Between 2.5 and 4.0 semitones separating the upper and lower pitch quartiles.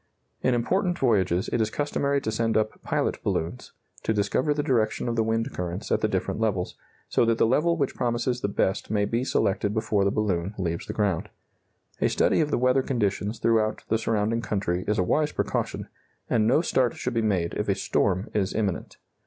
Yes: average, 3.4 semitones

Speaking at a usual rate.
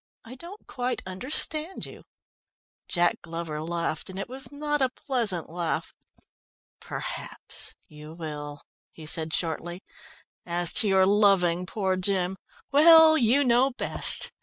No: slow, 130 wpm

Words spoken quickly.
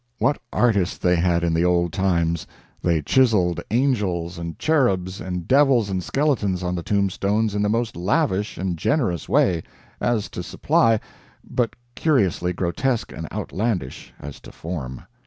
No: average, 150 wpm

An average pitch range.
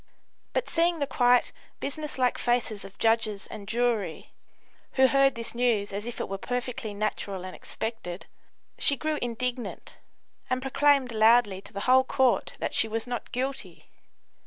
Yes: average, 3.4 semitones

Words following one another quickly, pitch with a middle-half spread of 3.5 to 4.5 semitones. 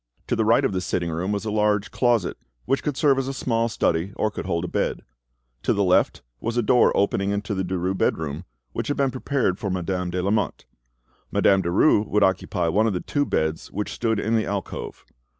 Yes: fast, 220 wpm; average, 3.8 semitones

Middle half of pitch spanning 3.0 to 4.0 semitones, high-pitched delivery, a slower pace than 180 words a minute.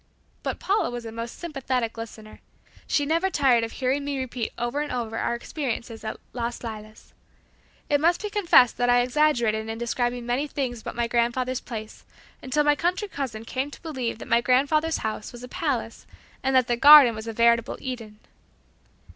No: average, 3.7 semitones; high, 245 Hz; average, 185 wpm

